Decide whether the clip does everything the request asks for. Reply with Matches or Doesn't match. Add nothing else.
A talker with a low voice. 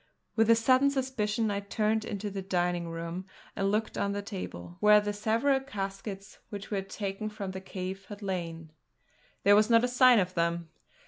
Doesn't match